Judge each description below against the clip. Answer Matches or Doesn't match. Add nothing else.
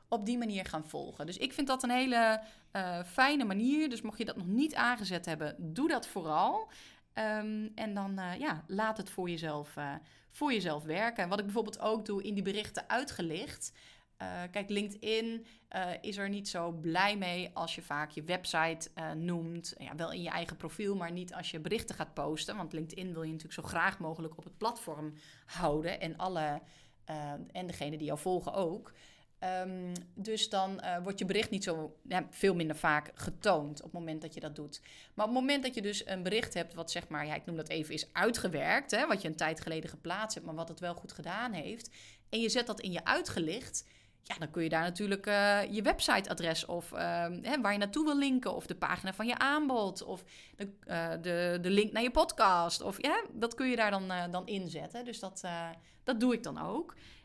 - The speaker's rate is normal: Doesn't match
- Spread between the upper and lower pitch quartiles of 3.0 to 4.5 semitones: Doesn't match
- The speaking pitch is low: Doesn't match